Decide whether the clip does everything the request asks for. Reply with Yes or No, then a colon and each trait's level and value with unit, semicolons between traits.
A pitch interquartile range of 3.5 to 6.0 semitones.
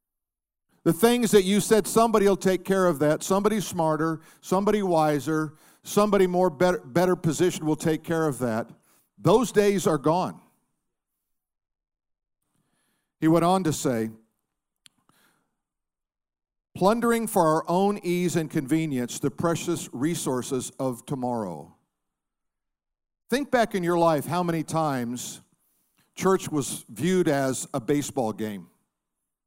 Yes: average, 5.3 semitones